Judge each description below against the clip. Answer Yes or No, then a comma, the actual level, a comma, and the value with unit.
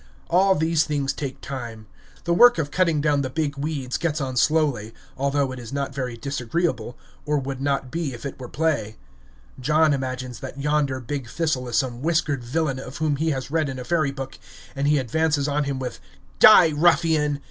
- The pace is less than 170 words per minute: No, average, 195 wpm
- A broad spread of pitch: No, average, 3.2 semitones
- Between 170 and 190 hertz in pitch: No, medium, 140 Hz